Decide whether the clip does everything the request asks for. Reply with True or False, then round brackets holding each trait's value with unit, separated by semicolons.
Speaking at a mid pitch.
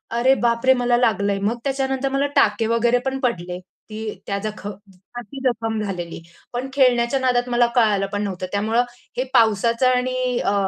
False (235 Hz)